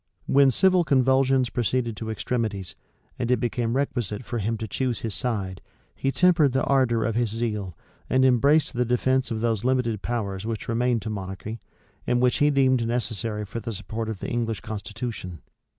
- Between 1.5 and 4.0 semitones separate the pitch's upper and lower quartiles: Yes, average, 3.0 semitones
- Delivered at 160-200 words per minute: Yes, average, 180 wpm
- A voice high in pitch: No, low, 115 Hz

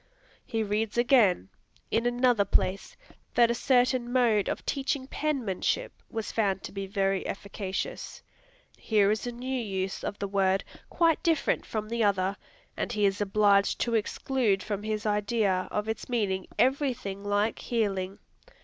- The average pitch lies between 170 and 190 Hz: No, high, 215 Hz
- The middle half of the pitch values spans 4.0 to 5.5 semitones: No, average, 3.6 semitones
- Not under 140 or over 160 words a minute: Yes, average, 155 wpm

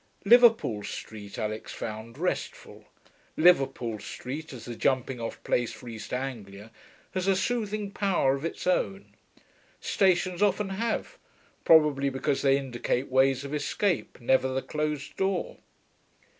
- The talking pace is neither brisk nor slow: No, slow, 130 wpm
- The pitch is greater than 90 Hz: Yes, medium, 140 Hz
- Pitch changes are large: Yes, wide, 7.3 semitones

